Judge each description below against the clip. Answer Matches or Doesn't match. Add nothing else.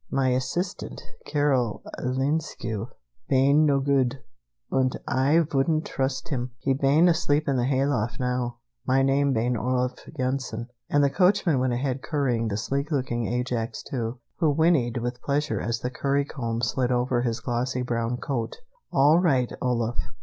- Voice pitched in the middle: Doesn't match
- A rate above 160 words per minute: Doesn't match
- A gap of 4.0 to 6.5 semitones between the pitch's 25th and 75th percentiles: Doesn't match